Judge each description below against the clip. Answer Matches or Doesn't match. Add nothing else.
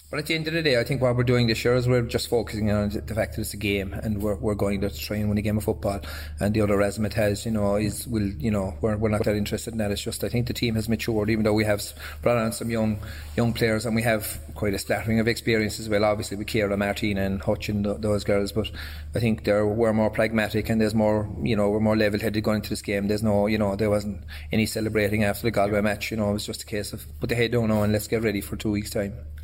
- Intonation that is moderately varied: Doesn't match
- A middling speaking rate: Doesn't match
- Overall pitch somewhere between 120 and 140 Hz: Doesn't match